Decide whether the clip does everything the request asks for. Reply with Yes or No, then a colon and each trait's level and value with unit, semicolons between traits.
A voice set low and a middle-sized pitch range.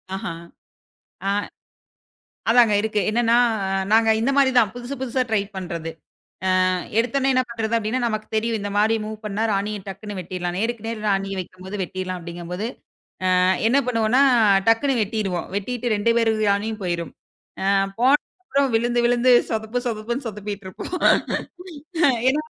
No: high, 220 Hz; average, 3.4 semitones